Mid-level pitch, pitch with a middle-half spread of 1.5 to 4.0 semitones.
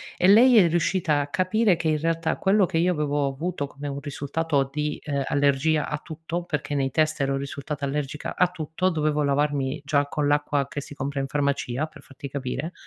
Yes: medium, 150 Hz; narrow, 2.5 semitones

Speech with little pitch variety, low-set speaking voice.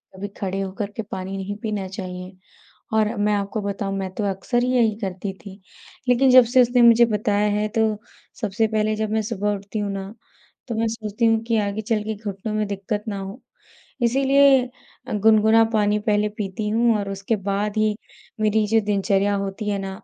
No: narrow, 2.0 semitones; high, 210 Hz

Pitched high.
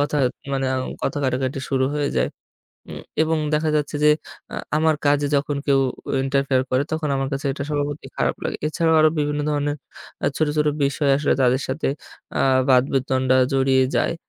No: medium, 140 Hz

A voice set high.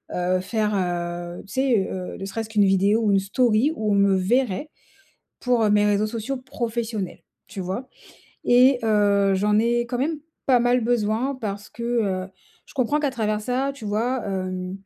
Yes: high, 215 Hz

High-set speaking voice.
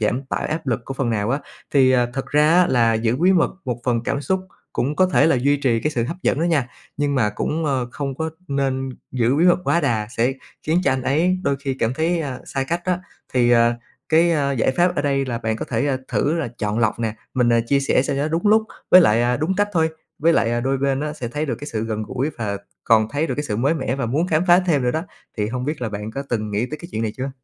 No: low, 135 Hz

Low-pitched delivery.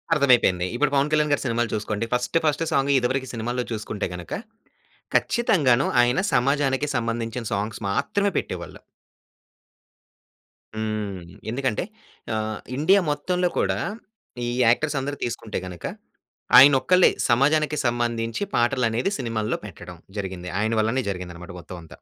Yes: low, 120 Hz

